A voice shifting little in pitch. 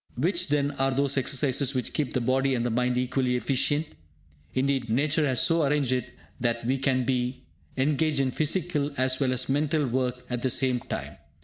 Yes: narrow, 2.3 semitones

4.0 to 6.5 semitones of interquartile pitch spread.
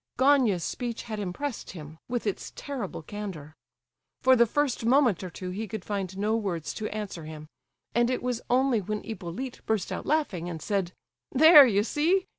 Yes: wide, 5.5 semitones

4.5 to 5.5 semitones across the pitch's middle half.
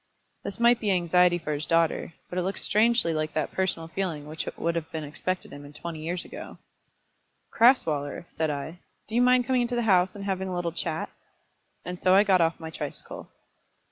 No: average, 3.6 semitones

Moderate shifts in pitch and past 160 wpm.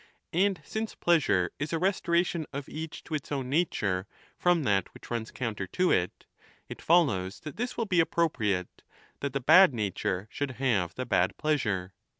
No: wide, 8.7 semitones; average, 170 wpm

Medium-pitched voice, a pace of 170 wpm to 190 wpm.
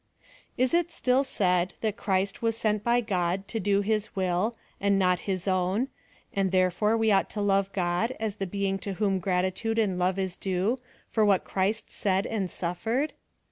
No: high, 200 Hz; average, 180 wpm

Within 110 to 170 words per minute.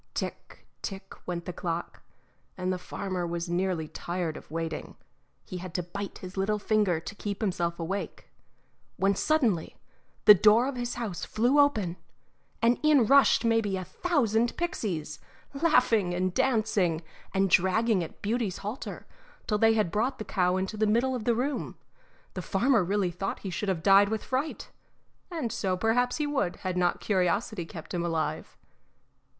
Yes: average, 165 wpm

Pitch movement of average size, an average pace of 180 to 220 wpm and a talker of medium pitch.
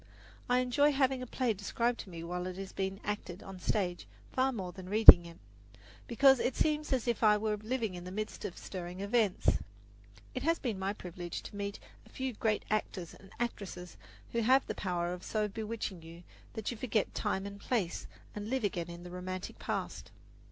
No: average, 4.6 semitones; fast, 205 wpm; high, 205 Hz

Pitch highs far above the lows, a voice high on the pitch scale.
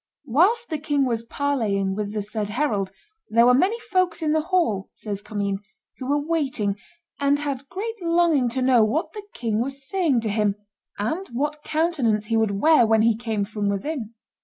Yes: wide, 6.5 semitones; very high, 255 Hz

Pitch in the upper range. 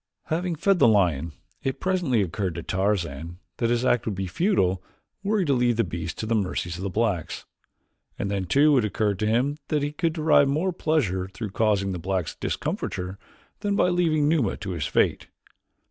No: low, 110 Hz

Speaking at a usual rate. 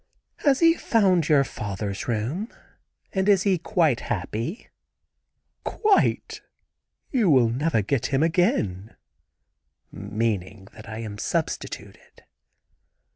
No: slow, 105 wpm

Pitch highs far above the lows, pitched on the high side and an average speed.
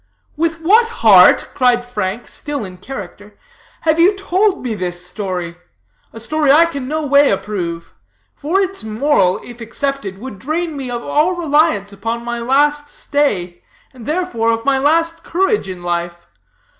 Yes: wide, 7.6 semitones; very high, 255 Hz; average, 155 wpm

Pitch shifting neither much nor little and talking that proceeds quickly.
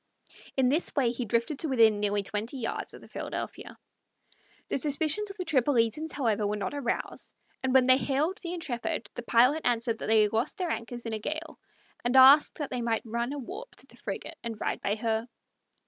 Yes: average, 4.4 semitones; fast, 210 wpm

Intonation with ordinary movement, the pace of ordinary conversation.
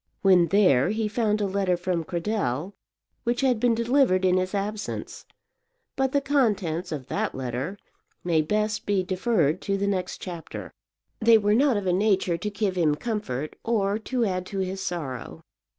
Yes: average, 3.6 semitones; average, 170 wpm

